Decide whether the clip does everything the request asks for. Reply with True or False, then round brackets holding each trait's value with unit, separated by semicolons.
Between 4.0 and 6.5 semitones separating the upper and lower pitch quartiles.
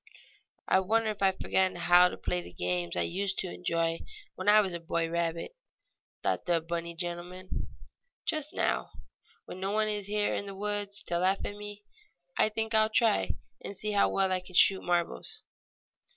False (3.3 semitones)